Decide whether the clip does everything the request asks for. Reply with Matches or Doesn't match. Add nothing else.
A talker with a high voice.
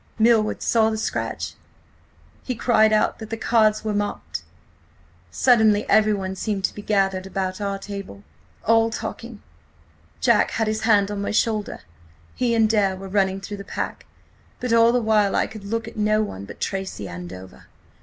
Matches